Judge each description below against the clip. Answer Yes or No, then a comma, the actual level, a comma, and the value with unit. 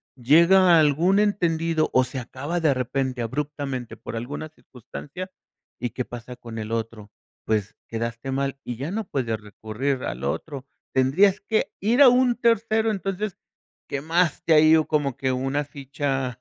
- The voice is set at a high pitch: No, medium, 140 Hz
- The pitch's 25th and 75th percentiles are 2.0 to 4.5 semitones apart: No, wide, 5.4 semitones